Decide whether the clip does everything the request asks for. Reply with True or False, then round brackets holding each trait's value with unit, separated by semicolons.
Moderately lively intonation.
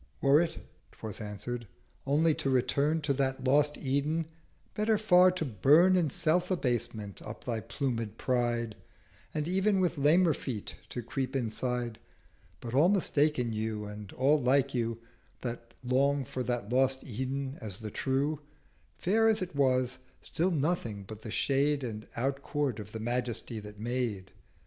True (4.3 semitones)